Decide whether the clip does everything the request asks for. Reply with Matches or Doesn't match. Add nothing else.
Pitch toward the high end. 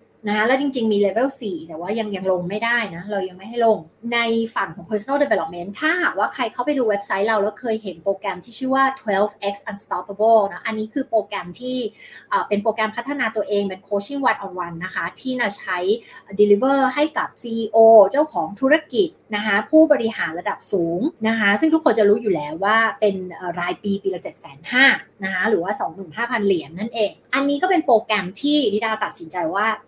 Matches